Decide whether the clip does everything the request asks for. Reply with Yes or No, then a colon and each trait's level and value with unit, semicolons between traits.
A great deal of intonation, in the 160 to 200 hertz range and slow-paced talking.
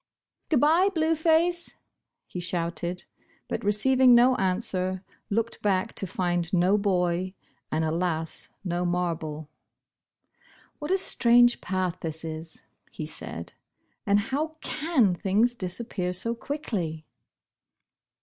Yes: wide, 5.8 semitones; high, 190 Hz; slow, 120 wpm